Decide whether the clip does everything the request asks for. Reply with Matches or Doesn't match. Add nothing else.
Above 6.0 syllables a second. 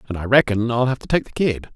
Matches